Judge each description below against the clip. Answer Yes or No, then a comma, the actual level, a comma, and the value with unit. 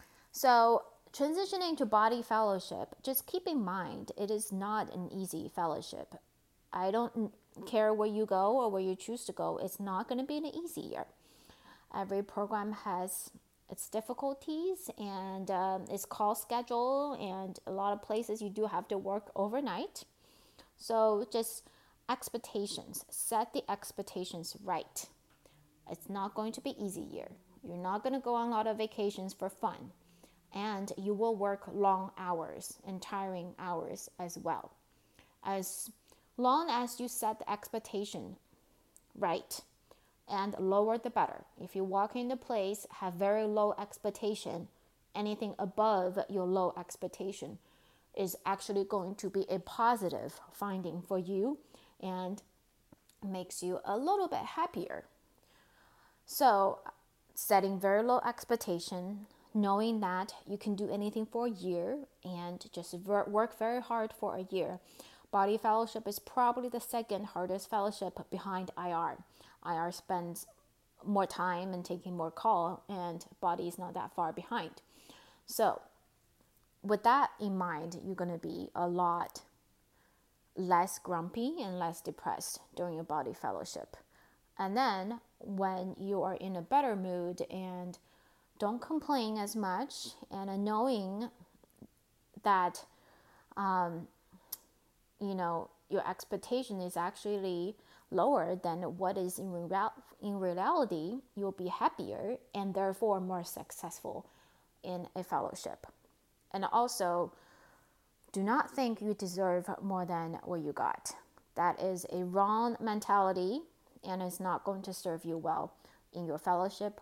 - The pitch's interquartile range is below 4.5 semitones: Yes, average, 3.3 semitones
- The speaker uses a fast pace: No, average, 140 wpm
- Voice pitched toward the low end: No, high, 200 Hz